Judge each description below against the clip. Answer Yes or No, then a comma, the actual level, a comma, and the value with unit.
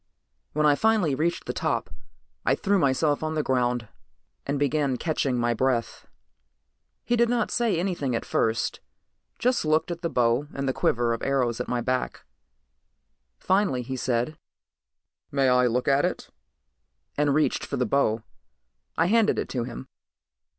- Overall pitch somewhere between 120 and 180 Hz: Yes, medium, 140 Hz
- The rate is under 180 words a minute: Yes, average, 155 wpm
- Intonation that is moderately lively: Yes, average, 4.7 semitones